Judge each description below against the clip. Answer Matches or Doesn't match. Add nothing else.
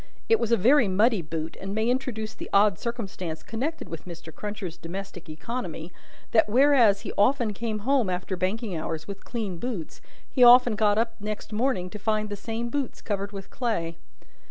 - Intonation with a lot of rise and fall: Doesn't match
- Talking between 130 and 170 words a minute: Doesn't match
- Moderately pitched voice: Doesn't match